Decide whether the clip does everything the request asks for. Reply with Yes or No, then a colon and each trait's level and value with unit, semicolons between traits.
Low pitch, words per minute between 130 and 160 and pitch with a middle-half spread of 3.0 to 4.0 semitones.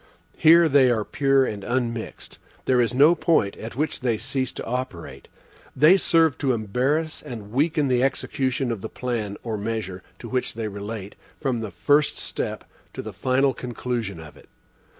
No: low, 125 Hz; average, 170 wpm; average, 3.7 semitones